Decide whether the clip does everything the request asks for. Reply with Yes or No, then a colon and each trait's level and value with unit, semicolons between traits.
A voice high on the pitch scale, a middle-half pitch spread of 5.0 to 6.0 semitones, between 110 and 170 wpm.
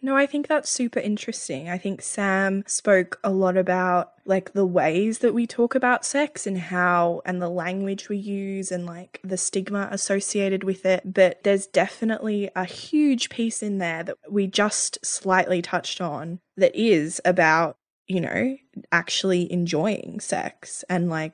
No: high, 195 Hz; average, 2.9 semitones; average, 165 wpm